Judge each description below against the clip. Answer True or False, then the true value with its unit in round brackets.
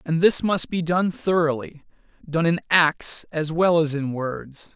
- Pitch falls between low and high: True (160 Hz)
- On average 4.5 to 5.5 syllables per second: False (3.9 syllables/s)